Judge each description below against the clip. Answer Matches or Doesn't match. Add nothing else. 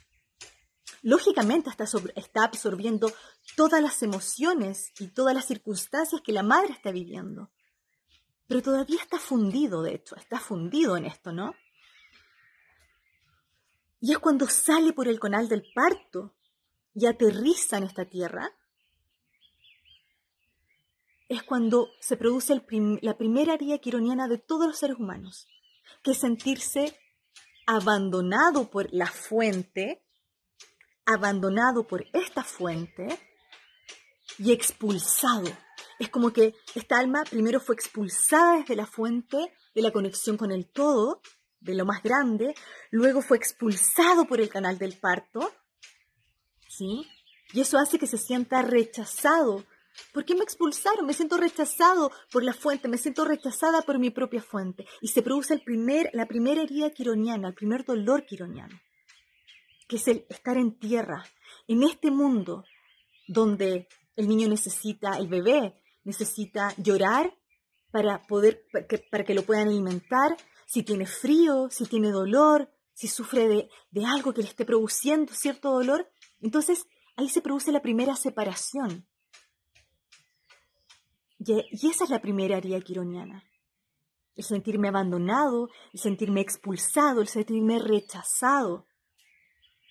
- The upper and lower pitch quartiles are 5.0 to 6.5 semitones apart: Matches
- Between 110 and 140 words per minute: Matches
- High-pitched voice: Matches